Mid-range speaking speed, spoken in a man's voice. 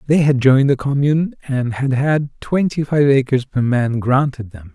Yes: average, 190 wpm; male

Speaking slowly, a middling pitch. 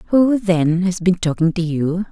No: average, 200 wpm; medium, 180 Hz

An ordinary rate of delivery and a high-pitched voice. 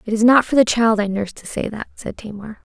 No: fast, 285 wpm; high, 220 Hz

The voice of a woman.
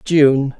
Yes: female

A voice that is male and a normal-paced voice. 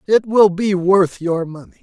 Yes: male; average, 195 wpm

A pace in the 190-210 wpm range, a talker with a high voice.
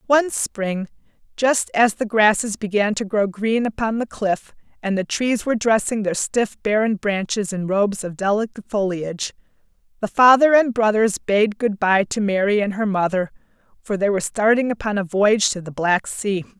No: average, 180 wpm; high, 210 Hz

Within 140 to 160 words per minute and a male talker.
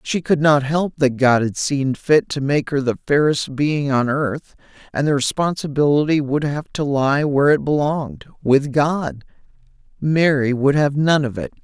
No: average, 175 wpm; male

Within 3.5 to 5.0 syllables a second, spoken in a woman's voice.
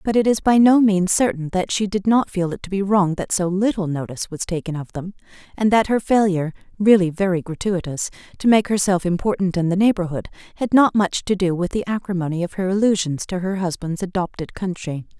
No: 5.5 syllables/s; female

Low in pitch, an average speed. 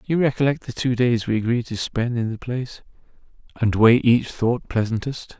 Yes: low, 120 Hz; average, 190 wpm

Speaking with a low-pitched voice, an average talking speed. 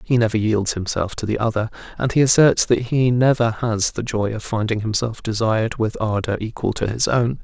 No: low, 110 Hz; fast, 210 wpm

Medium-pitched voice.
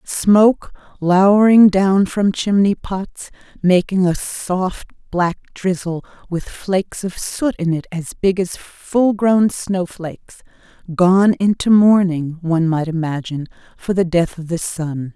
Yes: medium, 180 Hz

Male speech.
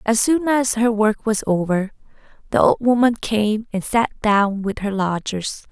No: female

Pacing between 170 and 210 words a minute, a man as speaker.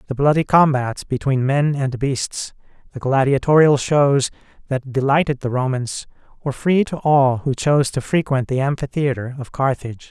No: average, 155 wpm; male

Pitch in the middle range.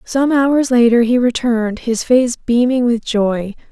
No: high, 240 Hz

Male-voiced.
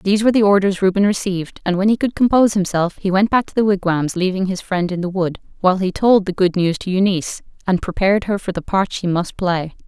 No: female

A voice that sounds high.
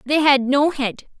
Yes: very high, 275 Hz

